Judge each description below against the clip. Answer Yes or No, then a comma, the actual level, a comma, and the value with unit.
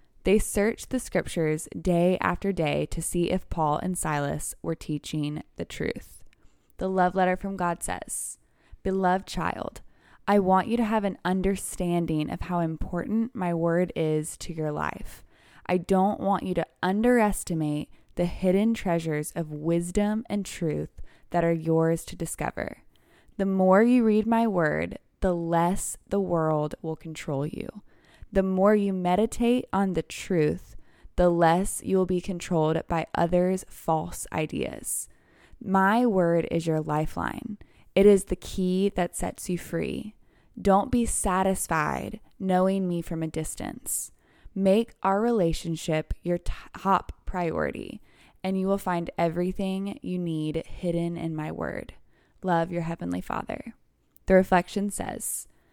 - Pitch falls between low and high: Yes, medium, 180 Hz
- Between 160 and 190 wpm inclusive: No, average, 145 wpm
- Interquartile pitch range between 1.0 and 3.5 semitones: Yes, average, 2.9 semitones